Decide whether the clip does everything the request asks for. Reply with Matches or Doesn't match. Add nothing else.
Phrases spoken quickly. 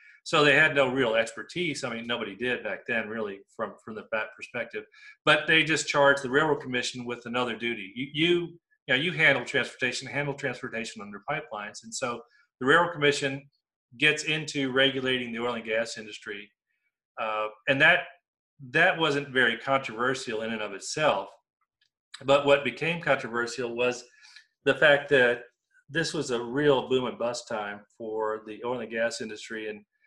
Doesn't match